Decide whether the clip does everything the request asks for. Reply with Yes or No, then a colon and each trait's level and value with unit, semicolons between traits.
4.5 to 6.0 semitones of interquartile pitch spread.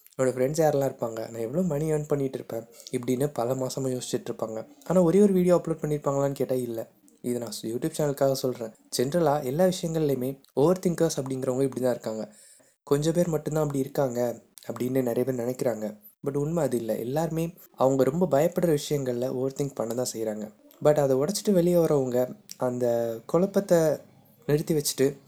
No: average, 3.9 semitones